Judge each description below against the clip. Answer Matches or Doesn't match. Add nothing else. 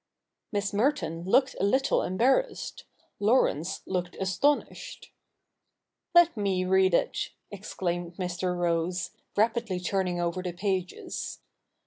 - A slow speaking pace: Matches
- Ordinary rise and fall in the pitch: Matches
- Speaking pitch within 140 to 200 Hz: Matches